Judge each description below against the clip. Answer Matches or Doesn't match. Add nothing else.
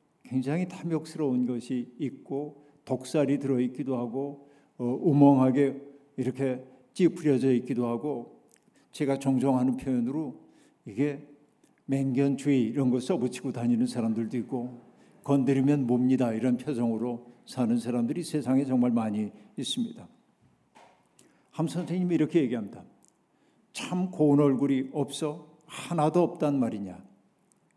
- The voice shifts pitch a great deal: Doesn't match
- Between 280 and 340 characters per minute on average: Matches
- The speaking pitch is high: Doesn't match